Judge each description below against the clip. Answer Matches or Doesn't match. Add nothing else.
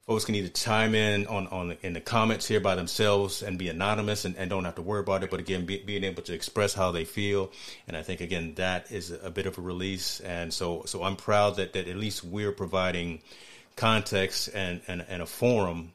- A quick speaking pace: Matches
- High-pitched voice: Doesn't match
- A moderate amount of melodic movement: Doesn't match